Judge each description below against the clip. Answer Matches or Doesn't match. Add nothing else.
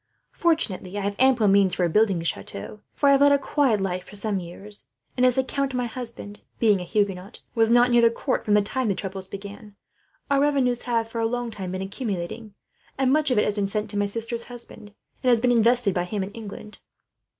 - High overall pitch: Matches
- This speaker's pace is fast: Matches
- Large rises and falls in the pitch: Doesn't match